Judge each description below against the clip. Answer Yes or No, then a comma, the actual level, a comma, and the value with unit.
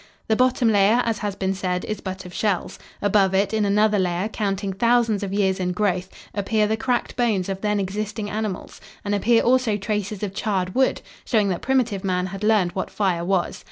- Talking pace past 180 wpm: Yes, average, 200 wpm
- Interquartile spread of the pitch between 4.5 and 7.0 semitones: No, narrow, 2.4 semitones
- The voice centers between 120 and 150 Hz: No, high, 205 Hz